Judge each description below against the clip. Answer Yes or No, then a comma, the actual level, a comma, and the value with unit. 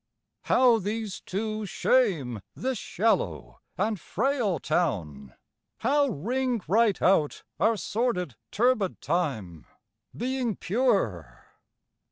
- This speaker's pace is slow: Yes, slow, 95 wpm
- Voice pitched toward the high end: Yes, high, 205 Hz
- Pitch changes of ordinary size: No, wide, 7.6 semitones